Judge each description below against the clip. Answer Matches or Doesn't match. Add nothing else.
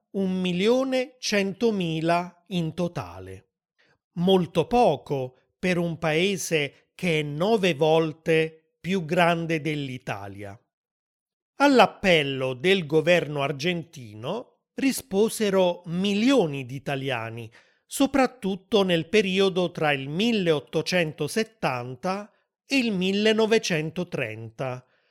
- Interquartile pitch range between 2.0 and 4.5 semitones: Doesn't match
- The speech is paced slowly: Matches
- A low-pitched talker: Doesn't match